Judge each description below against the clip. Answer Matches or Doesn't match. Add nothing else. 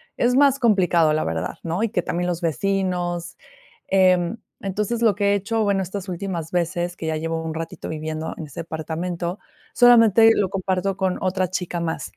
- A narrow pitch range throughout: Doesn't match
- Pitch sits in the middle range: Matches